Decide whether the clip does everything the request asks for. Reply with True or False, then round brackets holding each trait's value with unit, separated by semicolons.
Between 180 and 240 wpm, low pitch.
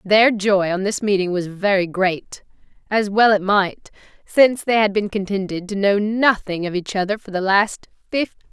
False (195 wpm; 200 Hz)